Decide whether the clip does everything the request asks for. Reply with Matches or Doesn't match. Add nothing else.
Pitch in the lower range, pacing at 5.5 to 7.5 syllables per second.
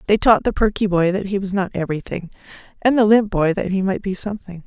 Doesn't match